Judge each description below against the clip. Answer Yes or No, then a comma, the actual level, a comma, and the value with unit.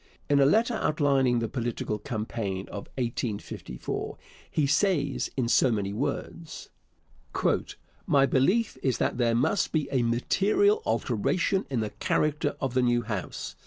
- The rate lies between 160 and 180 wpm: No, average, 140 wpm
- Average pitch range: Yes, average, 4.6 semitones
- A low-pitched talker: Yes, low, 130 Hz